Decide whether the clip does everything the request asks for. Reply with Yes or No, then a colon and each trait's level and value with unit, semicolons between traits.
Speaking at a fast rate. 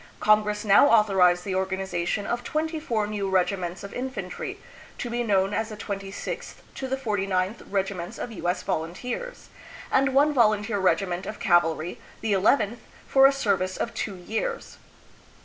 No: average, 165 wpm